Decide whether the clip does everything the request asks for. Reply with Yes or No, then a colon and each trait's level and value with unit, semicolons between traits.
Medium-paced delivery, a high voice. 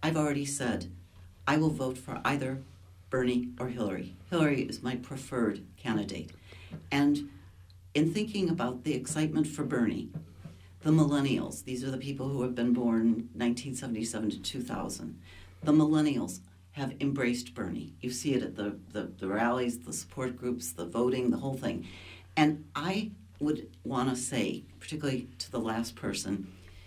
No: average, 155 wpm; low, 125 Hz